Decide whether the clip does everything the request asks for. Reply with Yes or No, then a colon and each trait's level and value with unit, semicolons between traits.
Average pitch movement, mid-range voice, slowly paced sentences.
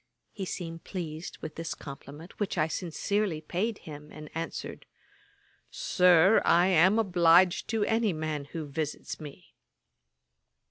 Yes: average, 3.5 semitones; medium, 165 Hz; slow, 130 wpm